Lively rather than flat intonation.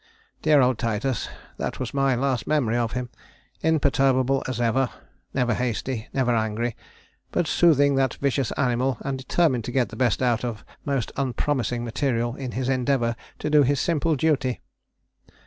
No: narrow, 2.5 semitones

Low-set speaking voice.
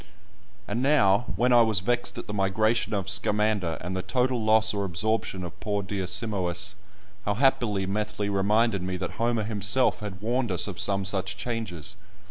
Yes: low, 105 Hz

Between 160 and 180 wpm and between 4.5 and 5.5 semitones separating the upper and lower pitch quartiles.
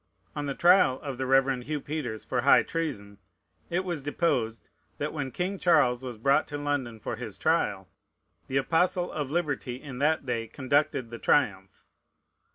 No: average, 165 wpm; average, 4.0 semitones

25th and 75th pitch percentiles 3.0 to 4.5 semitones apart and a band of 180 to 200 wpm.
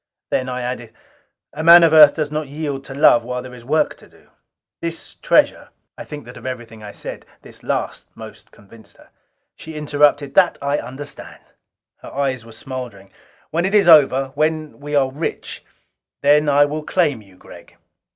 Yes: average, 3.4 semitones; average, 185 wpm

